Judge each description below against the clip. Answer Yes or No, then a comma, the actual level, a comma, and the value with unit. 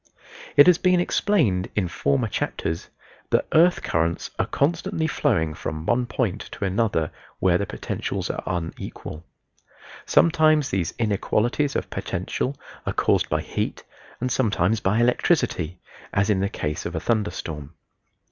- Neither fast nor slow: Yes, average, 145 wpm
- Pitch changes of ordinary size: No, wide, 8.1 semitones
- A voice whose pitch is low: Yes, low, 105 Hz